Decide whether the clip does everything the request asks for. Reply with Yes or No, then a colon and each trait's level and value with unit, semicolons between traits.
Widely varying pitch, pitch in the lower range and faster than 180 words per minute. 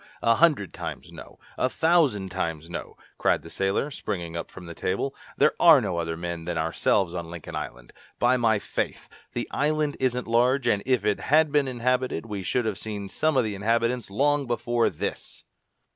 Yes: wide, 6.1 semitones; low, 115 Hz; average, 190 wpm